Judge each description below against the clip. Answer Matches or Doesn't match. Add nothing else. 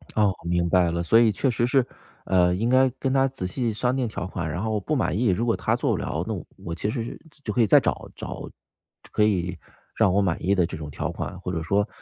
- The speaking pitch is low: Matches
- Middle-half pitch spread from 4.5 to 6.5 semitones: Matches